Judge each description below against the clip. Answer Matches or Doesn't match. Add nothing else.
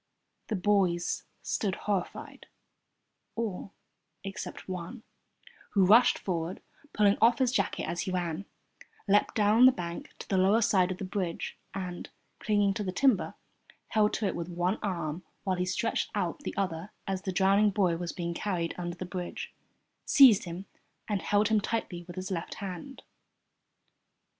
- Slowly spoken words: Doesn't match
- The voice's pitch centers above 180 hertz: Matches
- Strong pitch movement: Doesn't match